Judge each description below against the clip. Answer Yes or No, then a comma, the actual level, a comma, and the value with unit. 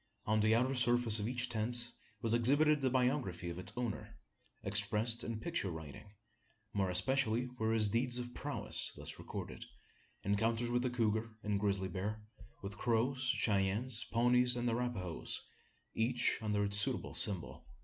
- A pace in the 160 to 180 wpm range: No, average, 150 wpm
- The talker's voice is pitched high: No, low, 115 Hz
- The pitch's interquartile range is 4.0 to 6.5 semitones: No, average, 3.0 semitones